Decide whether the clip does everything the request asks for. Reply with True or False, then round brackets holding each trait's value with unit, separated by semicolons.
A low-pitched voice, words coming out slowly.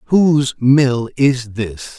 True (125 Hz; 120 wpm)